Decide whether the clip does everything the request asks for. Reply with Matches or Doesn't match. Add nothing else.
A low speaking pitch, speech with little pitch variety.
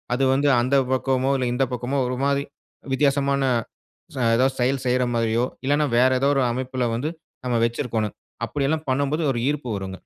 Matches